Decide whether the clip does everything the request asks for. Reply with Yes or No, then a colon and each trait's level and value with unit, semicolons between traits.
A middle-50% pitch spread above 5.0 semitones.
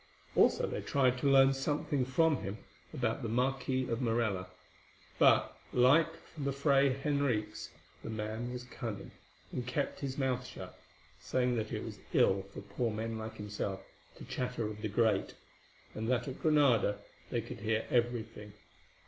No: average, 3.5 semitones